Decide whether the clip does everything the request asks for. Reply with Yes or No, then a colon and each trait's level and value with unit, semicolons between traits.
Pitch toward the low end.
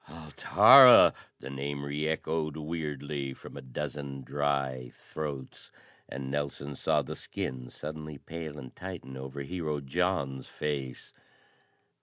Yes: very low, 70 Hz